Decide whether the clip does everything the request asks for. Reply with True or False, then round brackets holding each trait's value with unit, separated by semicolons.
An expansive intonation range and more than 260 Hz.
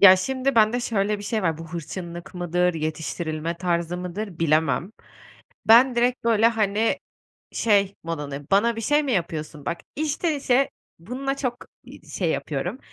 False (5.9 semitones; 195 Hz)